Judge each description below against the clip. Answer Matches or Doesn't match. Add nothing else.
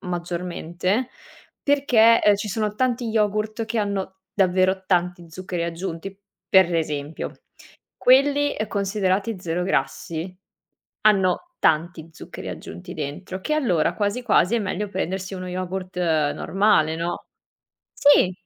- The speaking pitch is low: Doesn't match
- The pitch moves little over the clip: Doesn't match